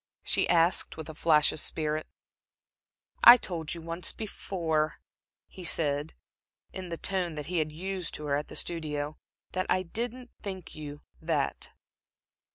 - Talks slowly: No, average, 155 wpm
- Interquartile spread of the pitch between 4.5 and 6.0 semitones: No, average, 3.3 semitones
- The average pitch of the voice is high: No, medium, 165 Hz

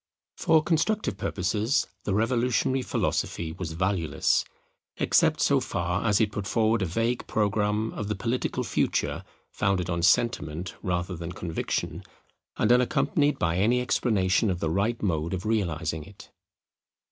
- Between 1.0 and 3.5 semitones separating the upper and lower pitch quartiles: No, average, 4.8 semitones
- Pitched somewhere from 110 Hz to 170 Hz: No, low, 100 Hz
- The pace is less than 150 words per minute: Yes, average, 140 wpm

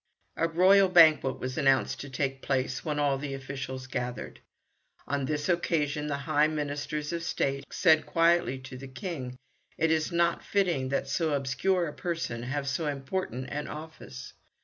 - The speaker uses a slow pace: No, average, 165 wpm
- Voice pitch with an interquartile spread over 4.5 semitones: No, average, 3.5 semitones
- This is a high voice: No, medium, 145 Hz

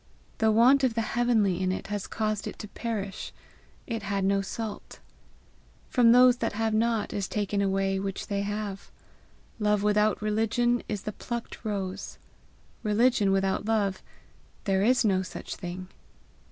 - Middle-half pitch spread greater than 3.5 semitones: No, narrow, 2.5 semitones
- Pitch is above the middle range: Yes, high, 210 Hz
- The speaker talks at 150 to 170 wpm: Yes, average, 155 wpm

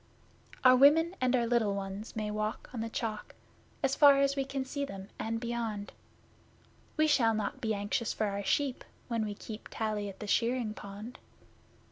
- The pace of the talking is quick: No, average, 180 wpm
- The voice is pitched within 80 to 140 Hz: No, high, 225 Hz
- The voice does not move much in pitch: No, average, 3.6 semitones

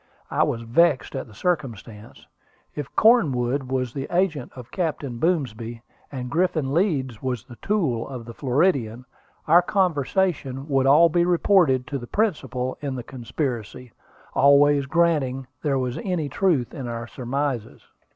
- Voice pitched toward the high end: No, low, 135 Hz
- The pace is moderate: Yes, average, 145 wpm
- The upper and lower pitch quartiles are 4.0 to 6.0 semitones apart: Yes, average, 5.1 semitones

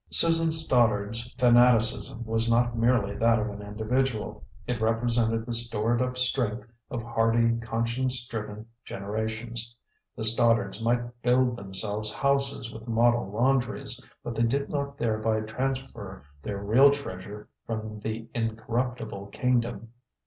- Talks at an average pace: No, slow, 125 wpm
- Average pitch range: No, narrow, 2.1 semitones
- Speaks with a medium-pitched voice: No, low, 115 Hz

